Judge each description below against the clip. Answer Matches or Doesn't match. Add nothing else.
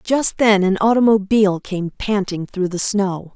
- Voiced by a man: Doesn't match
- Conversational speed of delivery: Matches